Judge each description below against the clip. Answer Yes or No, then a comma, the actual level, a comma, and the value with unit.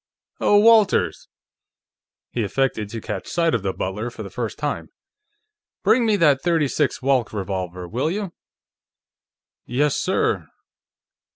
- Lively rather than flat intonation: Yes, wide, 8.1 semitones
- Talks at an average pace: No, slow, 125 wpm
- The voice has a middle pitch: No, low, 130 Hz